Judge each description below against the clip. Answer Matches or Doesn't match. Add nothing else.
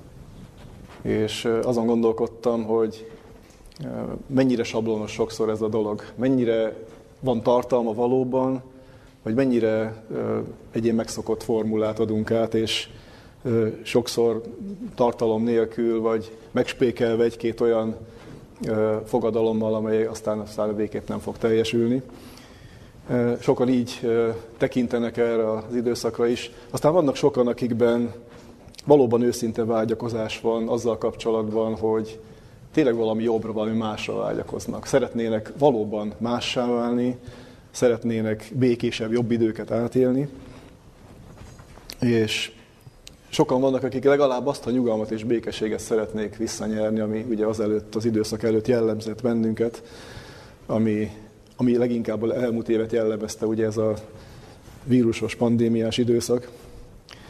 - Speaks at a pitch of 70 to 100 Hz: Doesn't match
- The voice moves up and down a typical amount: Doesn't match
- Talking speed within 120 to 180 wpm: Doesn't match